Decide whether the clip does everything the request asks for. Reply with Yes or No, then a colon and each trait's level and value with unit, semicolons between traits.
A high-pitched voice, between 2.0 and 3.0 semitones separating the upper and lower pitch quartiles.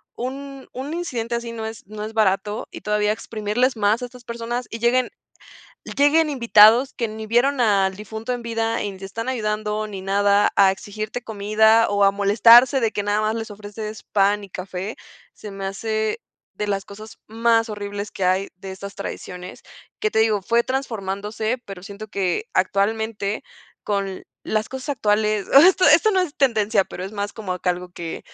Yes: high, 215 Hz; narrow, 2.6 semitones